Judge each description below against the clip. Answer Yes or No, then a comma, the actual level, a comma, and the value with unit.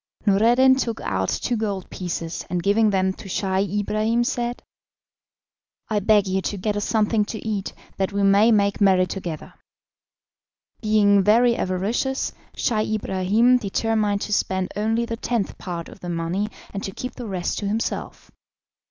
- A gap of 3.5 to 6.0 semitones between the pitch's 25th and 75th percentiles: No, average, 2.8 semitones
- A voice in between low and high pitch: No, high, 205 Hz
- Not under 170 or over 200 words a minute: No, average, 160 wpm